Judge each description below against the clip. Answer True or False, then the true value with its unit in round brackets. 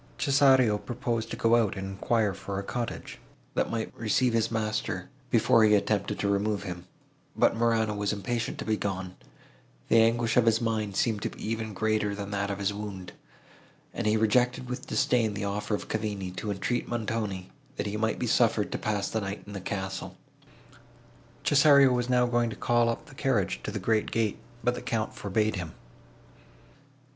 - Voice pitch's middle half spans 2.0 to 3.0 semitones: True (2.6 semitones)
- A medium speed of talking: True (190 wpm)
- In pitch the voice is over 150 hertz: False (110 Hz)